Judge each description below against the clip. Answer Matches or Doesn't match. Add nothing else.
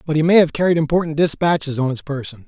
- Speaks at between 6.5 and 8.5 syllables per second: Matches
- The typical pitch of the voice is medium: Matches